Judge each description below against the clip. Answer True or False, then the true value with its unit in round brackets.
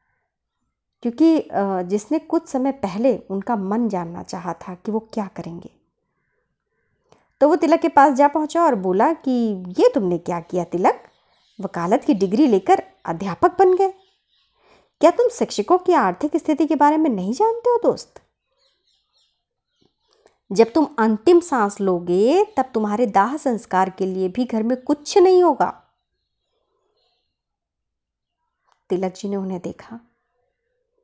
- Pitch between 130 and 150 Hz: False (265 Hz)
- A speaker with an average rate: True (135 wpm)